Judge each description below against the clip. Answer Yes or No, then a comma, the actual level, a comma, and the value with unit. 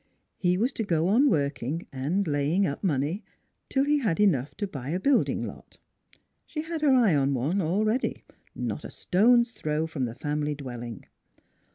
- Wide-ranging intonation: Yes, wide, 7.2 semitones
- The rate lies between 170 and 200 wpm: Yes, average, 175 wpm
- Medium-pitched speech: Yes, medium, 170 Hz